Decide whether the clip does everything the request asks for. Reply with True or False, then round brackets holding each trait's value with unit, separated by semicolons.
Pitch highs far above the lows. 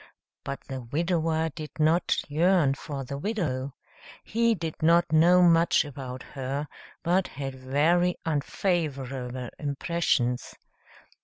False (4.1 semitones)